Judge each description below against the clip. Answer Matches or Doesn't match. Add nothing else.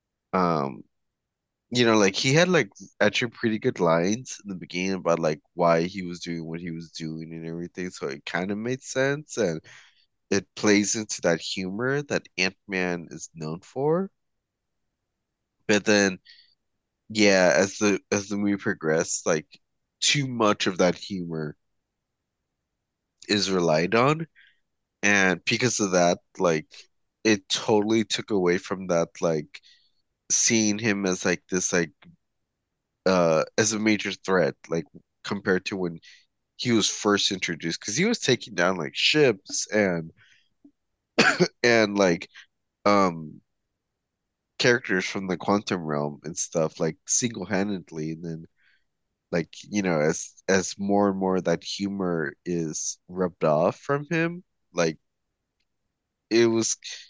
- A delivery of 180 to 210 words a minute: Doesn't match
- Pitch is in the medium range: Doesn't match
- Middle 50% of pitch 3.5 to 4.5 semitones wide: Matches